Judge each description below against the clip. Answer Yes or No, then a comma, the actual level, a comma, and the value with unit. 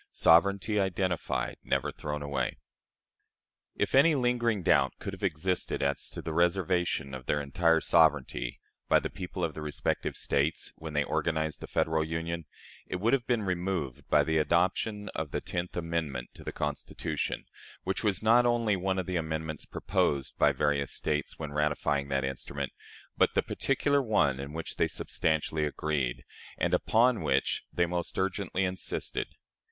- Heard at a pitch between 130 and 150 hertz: No, very low, 85 Hz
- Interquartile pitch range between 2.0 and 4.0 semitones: No, average, 4.4 semitones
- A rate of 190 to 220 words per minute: No, average, 160 wpm